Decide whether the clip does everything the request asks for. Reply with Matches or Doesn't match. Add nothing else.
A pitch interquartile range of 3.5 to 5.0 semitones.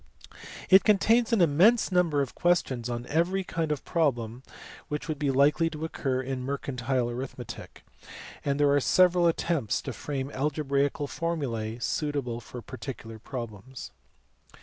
Matches